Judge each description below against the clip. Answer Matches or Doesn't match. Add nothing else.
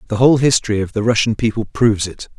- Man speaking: Matches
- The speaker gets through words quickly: Matches